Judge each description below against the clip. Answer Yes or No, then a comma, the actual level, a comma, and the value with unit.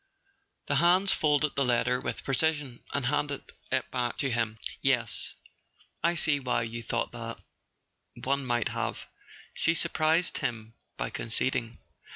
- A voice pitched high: No, low, 130 Hz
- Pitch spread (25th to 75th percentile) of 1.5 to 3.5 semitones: No, average, 3.9 semitones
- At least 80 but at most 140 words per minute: Yes, slow, 135 wpm